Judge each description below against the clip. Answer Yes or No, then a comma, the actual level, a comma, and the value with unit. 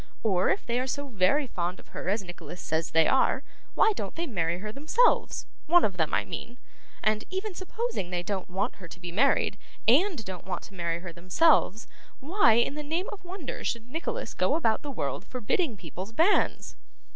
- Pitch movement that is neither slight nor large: No, wide, 9.0 semitones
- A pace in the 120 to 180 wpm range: No, average, 200 wpm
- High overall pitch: Yes, high, 225 Hz